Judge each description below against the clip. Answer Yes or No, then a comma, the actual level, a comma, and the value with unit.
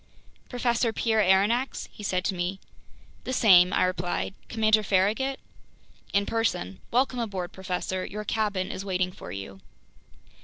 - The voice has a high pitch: Yes, high, 200 Hz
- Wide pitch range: No, average, 3.6 semitones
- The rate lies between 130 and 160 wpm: Yes, average, 140 wpm